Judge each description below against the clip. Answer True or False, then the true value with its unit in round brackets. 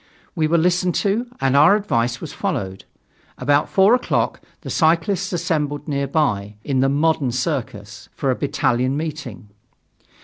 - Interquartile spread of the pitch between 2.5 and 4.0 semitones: False (4.7 semitones)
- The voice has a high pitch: False (145 Hz)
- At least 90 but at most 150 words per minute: True (140 wpm)